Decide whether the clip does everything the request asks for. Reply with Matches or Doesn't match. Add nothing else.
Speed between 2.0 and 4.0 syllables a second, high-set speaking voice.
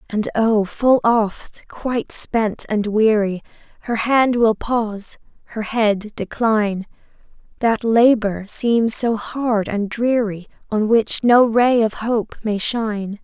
Matches